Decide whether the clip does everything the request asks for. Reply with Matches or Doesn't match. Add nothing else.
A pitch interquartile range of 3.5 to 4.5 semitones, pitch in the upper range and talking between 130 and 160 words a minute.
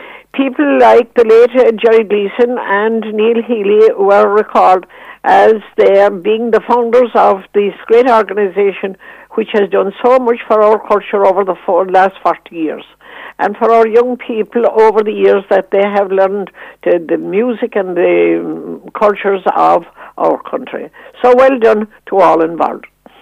Doesn't match